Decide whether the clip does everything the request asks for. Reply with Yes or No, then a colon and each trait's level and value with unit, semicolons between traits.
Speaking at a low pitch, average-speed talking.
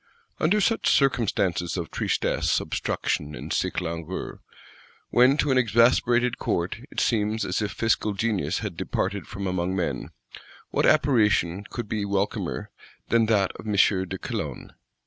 Yes: low, 105 Hz; average, 145 wpm